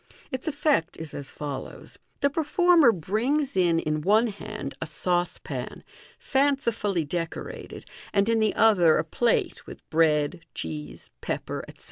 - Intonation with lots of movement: Yes, wide, 7.6 semitones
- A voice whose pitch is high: Yes, high, 195 Hz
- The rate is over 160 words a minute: No, average, 150 wpm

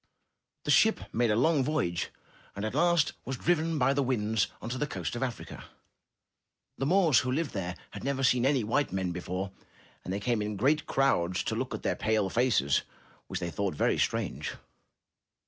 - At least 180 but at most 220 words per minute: Yes, average, 190 wpm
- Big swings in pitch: Yes, wide, 6.1 semitones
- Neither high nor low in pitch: No, low, 120 Hz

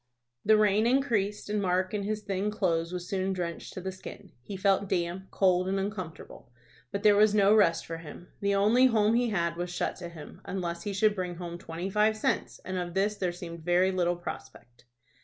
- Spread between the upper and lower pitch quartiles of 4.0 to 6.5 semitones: No, average, 3.0 semitones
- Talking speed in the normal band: No, fast, 210 wpm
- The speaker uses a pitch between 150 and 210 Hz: Yes, high, 190 Hz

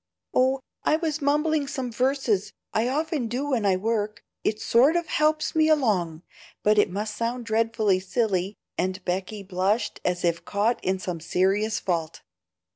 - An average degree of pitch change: No, wide, 5.9 semitones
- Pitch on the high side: Yes, high, 220 Hz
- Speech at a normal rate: Yes, average, 160 wpm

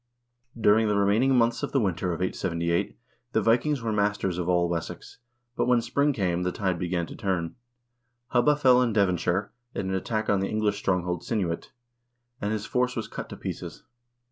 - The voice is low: Yes, low, 100 Hz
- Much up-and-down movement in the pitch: No, average, 4.5 semitones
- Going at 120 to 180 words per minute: No, average, 190 wpm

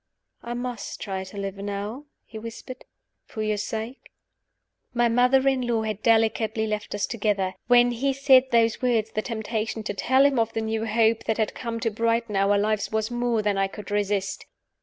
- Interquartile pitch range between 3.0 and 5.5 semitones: No, narrow, 2.5 semitones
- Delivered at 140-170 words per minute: No, average, 190 wpm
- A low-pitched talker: No, high, 220 Hz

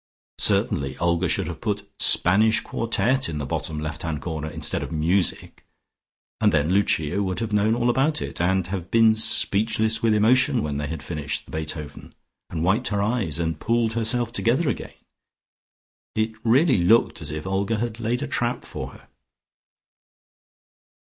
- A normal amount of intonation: No, wide, 5.9 semitones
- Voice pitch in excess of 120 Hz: No, low, 100 Hz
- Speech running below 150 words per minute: No, average, 165 wpm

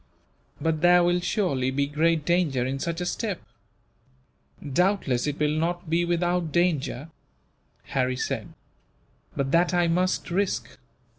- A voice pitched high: No, medium, 165 Hz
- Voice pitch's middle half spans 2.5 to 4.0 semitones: Yes, average, 3.6 semitones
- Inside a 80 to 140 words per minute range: Yes, slow, 135 wpm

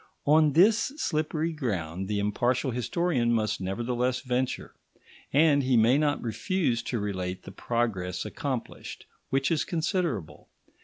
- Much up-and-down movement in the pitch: Yes, wide, 6.2 semitones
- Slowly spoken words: Yes, slow, 125 wpm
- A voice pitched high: No, low, 125 Hz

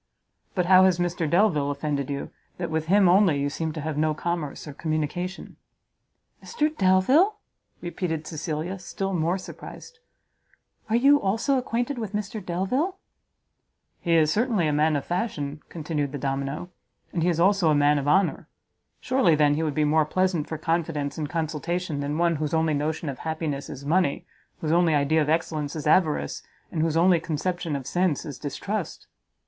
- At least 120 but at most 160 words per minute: No, average, 175 wpm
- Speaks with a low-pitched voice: No, medium, 165 Hz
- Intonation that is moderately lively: Yes, average, 3.8 semitones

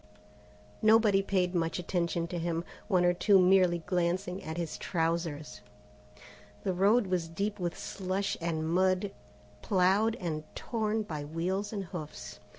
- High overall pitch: No, medium, 180 Hz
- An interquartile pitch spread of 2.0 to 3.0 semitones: Yes, average, 2.7 semitones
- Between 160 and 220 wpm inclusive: No, average, 140 wpm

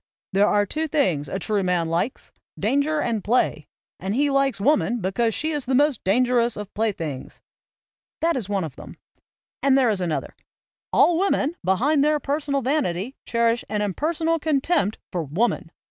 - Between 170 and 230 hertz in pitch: No, high, 240 Hz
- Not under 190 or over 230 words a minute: No, average, 175 wpm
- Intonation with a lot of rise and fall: Yes, wide, 6.8 semitones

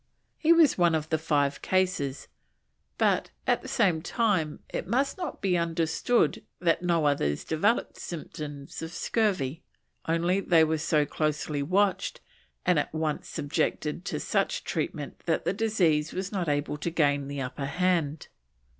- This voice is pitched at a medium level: Yes, medium, 160 Hz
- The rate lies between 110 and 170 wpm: Yes, average, 155 wpm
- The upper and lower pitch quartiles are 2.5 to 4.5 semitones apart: Yes, average, 3.8 semitones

